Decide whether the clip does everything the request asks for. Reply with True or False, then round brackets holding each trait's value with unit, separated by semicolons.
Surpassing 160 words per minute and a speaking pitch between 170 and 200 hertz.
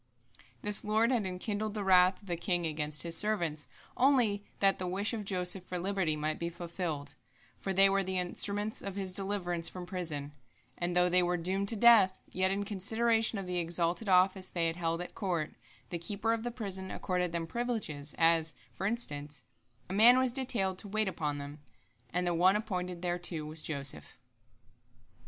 True (185 wpm; 185 Hz)